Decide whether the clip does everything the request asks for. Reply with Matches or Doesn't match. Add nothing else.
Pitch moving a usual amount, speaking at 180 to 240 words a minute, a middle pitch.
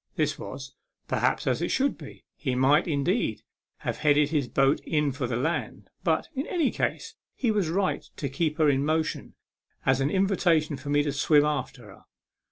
Matches